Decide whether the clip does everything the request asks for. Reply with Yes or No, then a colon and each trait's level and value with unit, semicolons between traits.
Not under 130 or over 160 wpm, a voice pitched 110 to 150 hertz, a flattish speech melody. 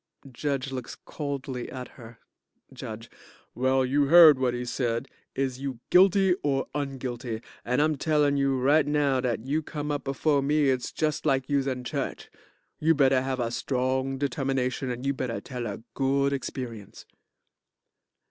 Yes: average, 155 wpm; low, 135 Hz; narrow, 2.2 semitones